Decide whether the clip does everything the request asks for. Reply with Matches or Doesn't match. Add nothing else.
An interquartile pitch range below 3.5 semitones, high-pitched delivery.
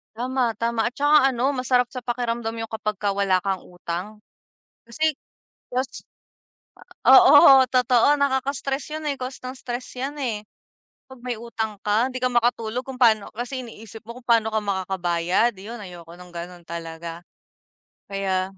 Doesn't match